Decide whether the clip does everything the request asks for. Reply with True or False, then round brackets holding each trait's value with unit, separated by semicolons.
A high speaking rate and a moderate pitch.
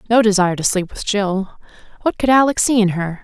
False (220 wpm; 205 Hz)